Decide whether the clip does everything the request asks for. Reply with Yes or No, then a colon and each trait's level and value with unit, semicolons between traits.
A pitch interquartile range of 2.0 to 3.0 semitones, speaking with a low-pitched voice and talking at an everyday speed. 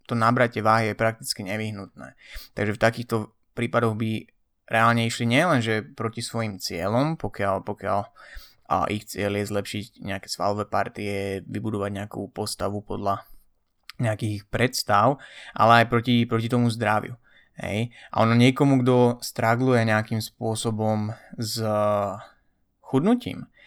Yes: narrow, 2.5 semitones; low, 110 Hz; average, 125 wpm